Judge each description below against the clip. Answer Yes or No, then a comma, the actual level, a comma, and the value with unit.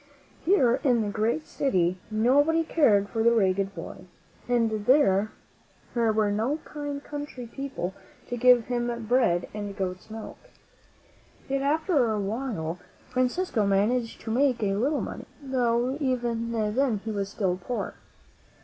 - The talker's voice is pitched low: No, high, 235 Hz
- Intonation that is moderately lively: Yes, average, 4.3 semitones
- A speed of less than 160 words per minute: Yes, average, 140 wpm